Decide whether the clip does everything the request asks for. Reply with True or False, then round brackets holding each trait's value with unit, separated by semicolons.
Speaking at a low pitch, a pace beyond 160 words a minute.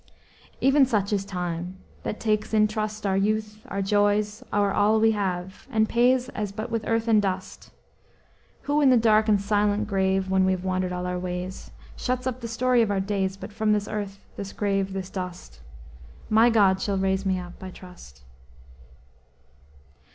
False (205 Hz; 180 wpm)